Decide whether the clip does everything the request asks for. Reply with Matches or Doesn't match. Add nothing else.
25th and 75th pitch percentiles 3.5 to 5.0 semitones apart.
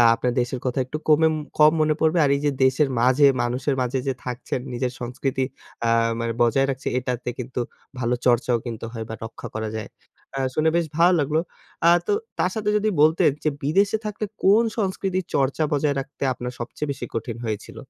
Matches